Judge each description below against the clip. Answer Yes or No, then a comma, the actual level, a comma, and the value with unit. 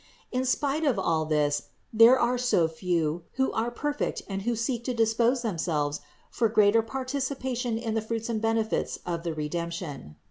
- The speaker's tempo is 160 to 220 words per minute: Yes, average, 170 wpm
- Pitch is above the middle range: Yes, high, 225 Hz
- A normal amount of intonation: No, wide, 6.5 semitones